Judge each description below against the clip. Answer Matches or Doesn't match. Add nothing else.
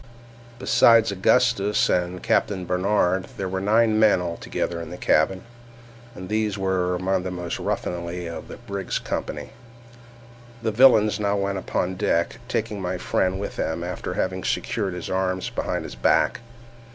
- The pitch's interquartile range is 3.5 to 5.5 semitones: Doesn't match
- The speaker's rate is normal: Matches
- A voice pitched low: Matches